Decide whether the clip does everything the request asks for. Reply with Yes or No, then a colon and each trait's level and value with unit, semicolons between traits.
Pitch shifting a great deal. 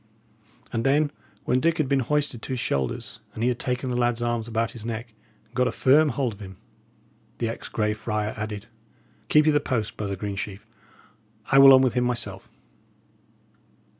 No: average, 3.5 semitones